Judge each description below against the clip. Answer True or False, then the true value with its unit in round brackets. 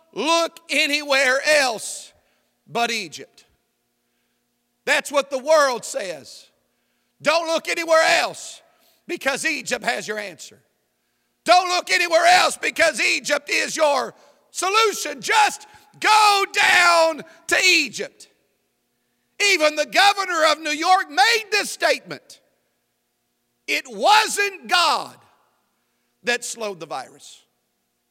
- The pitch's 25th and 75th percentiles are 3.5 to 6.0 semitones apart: True (4.6 semitones)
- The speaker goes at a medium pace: False (105 wpm)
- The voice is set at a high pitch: True (325 Hz)